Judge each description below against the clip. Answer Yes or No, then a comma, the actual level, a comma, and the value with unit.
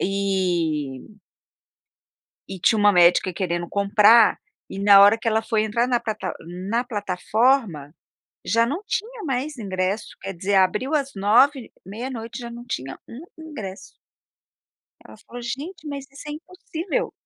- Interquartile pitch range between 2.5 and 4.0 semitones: No, average, 5.3 semitones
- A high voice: Yes, high, 220 Hz